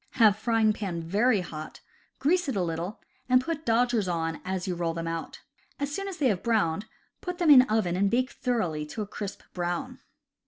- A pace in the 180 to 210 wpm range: Yes, average, 200 wpm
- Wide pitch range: Yes, wide, 6.3 semitones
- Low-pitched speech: No, high, 210 Hz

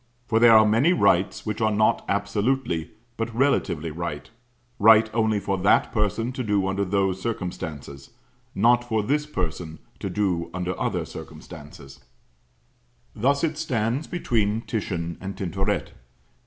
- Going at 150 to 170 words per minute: No, average, 140 wpm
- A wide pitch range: No, average, 4.1 semitones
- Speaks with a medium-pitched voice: No, low, 105 Hz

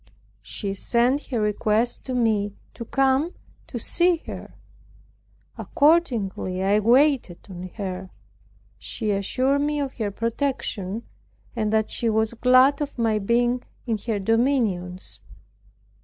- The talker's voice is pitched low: No, high, 230 Hz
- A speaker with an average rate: No, slow, 125 wpm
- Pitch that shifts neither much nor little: Yes, average, 4.4 semitones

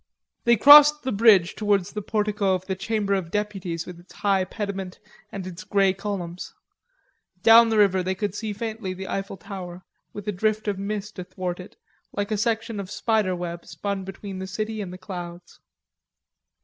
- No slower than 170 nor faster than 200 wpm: Yes, average, 180 wpm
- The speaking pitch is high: Yes, high, 200 Hz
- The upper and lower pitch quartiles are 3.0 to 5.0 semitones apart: No, narrow, 2.4 semitones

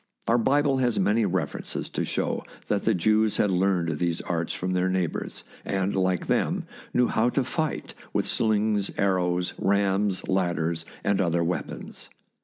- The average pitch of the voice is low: Yes, very low, 95 Hz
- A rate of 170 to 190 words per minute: No, average, 160 wpm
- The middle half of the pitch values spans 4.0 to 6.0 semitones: No, average, 3.5 semitones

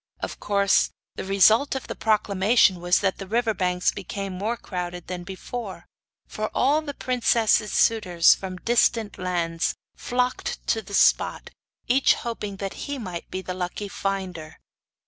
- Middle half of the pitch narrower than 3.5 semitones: No, average, 3.9 semitones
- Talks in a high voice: Yes, high, 200 Hz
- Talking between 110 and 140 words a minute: No, average, 150 wpm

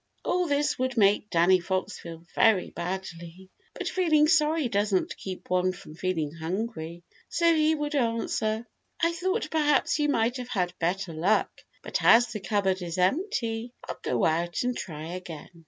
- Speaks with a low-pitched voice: No, high, 205 Hz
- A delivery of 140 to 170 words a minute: Yes, average, 165 wpm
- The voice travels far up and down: Yes, wide, 7.4 semitones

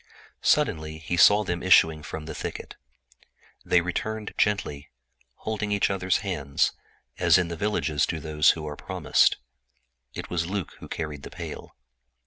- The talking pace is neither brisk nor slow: Yes, average, 150 wpm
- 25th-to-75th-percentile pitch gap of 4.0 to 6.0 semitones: Yes, average, 4.3 semitones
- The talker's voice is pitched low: Yes, very low, 85 Hz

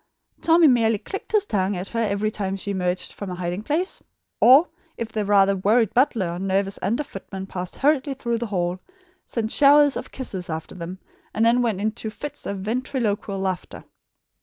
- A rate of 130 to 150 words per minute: No, average, 185 wpm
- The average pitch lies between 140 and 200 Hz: No, high, 210 Hz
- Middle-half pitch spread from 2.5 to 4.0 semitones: No, average, 4.5 semitones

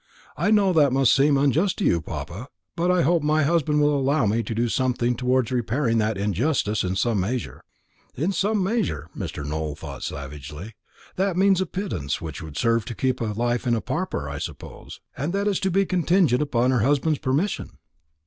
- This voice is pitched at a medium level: No, low, 130 Hz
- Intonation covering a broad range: Yes, wide, 7.3 semitones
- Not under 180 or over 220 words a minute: Yes, average, 195 wpm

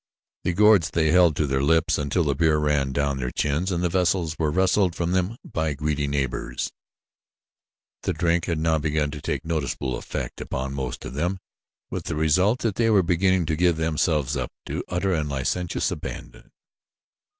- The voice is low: Yes, very low, 80 Hz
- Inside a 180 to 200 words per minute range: Yes, average, 185 wpm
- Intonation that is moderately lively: Yes, average, 3.5 semitones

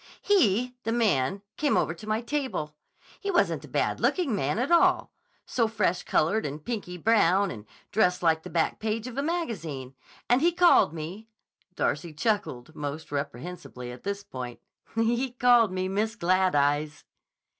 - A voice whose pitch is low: No, high, 200 Hz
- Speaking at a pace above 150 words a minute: No, average, 145 wpm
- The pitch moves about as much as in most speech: No, wide, 7.3 semitones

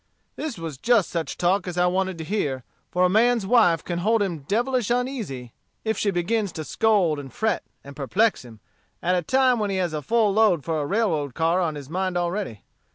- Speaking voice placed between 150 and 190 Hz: Yes, medium, 185 Hz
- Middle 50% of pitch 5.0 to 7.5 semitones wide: Yes, average, 5.3 semitones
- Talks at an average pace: No, fast, 215 wpm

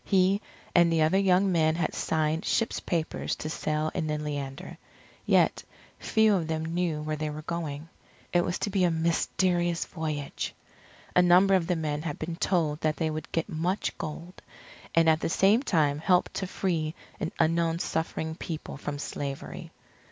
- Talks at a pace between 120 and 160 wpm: No, average, 175 wpm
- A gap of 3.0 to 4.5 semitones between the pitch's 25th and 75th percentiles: No, narrow, 2.5 semitones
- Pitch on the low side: No, medium, 165 Hz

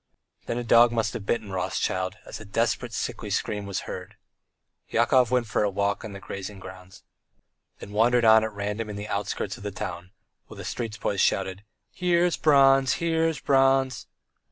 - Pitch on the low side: Yes, low, 110 Hz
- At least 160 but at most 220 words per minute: Yes, average, 180 wpm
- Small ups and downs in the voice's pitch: No, average, 3.9 semitones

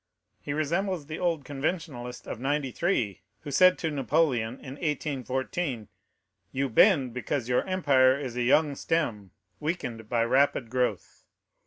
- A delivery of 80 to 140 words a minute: Yes, slow, 135 wpm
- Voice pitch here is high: No, medium, 140 Hz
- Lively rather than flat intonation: No, average, 4.1 semitones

